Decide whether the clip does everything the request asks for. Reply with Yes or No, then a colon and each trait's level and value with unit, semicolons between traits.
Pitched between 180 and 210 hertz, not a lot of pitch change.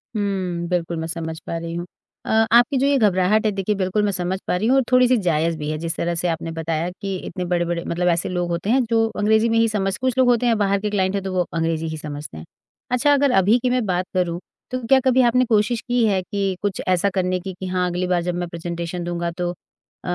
No: medium, 185 Hz; average, 4.1 semitones